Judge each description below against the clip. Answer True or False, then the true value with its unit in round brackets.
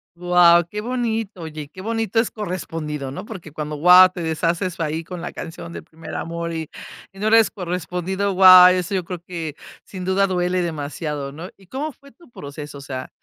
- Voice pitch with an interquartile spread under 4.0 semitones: True (3.1 semitones)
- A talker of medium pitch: True (180 Hz)